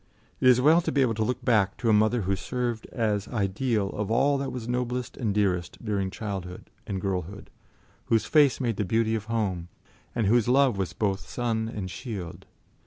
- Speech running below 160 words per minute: No, average, 195 wpm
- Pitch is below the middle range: Yes, low, 110 Hz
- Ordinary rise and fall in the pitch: Yes, average, 3.8 semitones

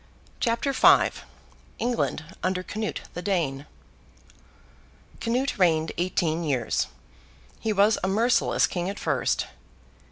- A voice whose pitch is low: No, high, 190 Hz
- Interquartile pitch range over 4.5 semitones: Yes, average, 5.0 semitones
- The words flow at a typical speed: No, slow, 105 wpm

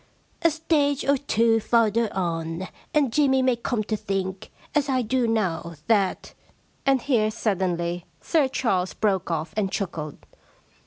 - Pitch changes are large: Yes, wide, 5.9 semitones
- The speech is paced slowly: No, average, 155 wpm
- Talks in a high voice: Yes, high, 220 Hz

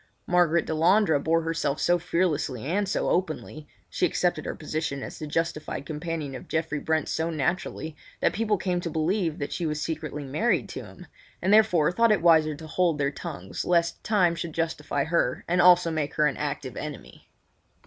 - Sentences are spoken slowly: No, average, 180 wpm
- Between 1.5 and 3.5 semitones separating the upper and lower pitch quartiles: Yes, average, 2.8 semitones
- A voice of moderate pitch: Yes, medium, 160 Hz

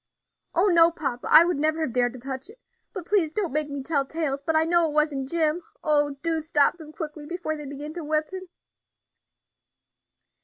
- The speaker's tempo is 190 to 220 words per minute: Yes, average, 200 wpm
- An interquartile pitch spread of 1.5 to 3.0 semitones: Yes, average, 2.7 semitones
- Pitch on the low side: No, very high, 310 Hz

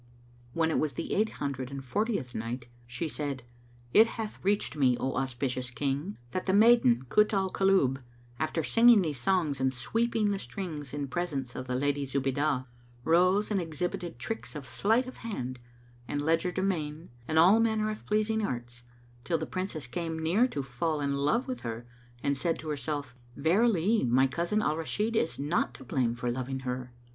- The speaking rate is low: No, average, 175 wpm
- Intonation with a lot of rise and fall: Yes, wide, 6.8 semitones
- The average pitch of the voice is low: No, medium, 155 Hz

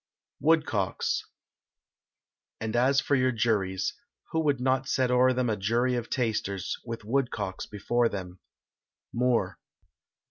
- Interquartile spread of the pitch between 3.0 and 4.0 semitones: Yes, average, 3.7 semitones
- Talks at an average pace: No, slow, 120 wpm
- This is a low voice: Yes, low, 120 Hz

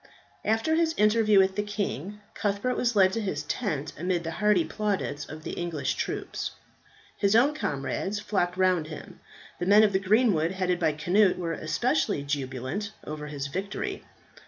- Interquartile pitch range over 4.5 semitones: Yes, average, 5.1 semitones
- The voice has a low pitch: No, high, 190 Hz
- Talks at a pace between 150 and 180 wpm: Yes, average, 165 wpm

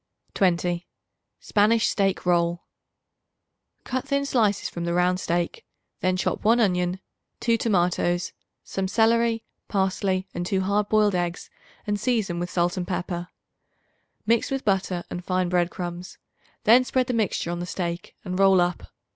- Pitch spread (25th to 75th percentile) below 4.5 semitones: Yes, average, 3.5 semitones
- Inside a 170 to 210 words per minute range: No, average, 150 wpm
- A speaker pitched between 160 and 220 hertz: Yes, medium, 185 Hz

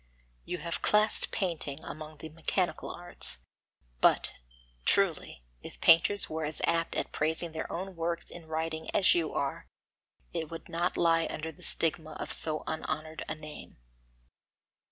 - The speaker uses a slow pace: No, average, 150 wpm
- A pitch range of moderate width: No, narrow, 1.5 semitones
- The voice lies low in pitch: No, medium, 160 Hz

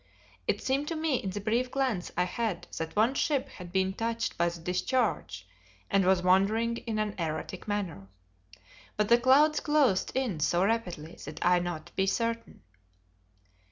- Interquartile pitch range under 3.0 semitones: No, average, 5.1 semitones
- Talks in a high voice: Yes, high, 205 Hz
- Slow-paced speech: No, average, 165 wpm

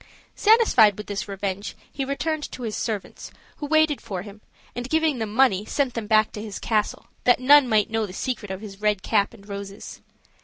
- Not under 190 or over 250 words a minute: Yes, average, 200 wpm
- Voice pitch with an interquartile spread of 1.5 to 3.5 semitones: No, average, 4.7 semitones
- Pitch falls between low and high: No, high, 220 Hz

